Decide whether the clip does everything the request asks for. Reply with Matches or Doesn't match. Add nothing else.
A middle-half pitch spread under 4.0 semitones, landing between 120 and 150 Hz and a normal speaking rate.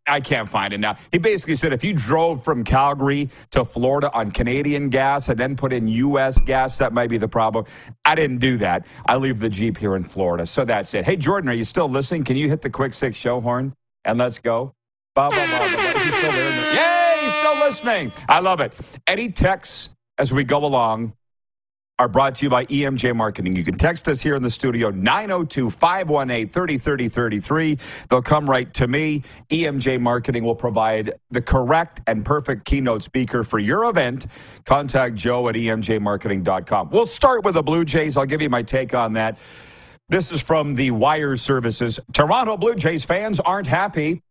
Doesn't match